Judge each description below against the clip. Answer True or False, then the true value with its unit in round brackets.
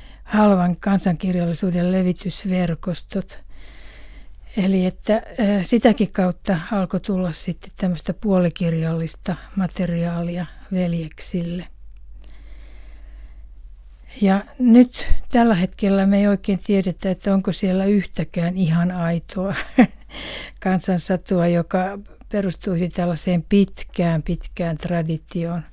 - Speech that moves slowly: True (80 wpm)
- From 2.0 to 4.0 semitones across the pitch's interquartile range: True (2.5 semitones)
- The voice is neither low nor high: True (180 Hz)